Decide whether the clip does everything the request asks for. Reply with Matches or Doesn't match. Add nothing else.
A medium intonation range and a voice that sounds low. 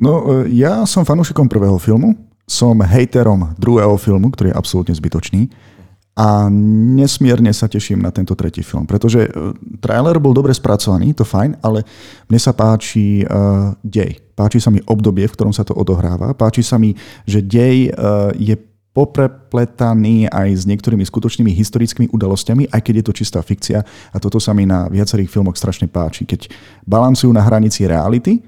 Matches